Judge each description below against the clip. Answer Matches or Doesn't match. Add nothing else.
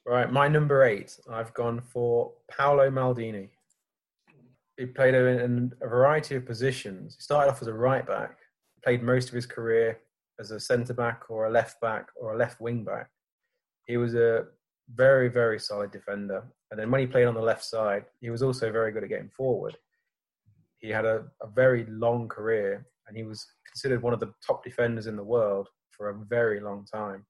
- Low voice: Matches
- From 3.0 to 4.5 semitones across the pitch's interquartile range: Doesn't match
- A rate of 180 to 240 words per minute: Matches